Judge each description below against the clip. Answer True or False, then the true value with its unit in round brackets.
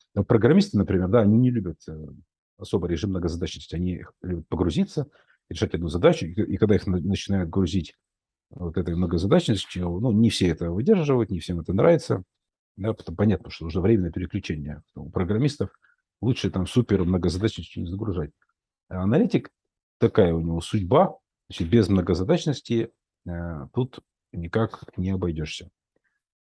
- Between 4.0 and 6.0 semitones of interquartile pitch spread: True (4.3 semitones)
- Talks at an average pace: True (140 wpm)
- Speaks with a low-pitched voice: True (95 Hz)